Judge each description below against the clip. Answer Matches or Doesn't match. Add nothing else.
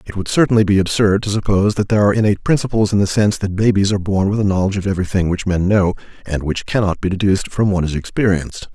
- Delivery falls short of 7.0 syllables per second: Doesn't match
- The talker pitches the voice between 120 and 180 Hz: Doesn't match